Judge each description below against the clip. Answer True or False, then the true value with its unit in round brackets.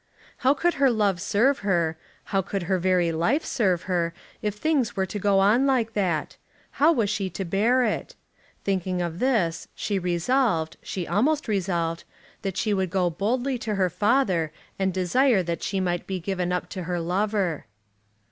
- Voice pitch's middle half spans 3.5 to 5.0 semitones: True (4.3 semitones)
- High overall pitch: True (195 Hz)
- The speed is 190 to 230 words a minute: False (175 wpm)